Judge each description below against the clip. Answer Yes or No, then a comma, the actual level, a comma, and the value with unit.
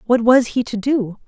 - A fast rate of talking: Yes, fast, 235 wpm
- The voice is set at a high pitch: Yes, high, 235 Hz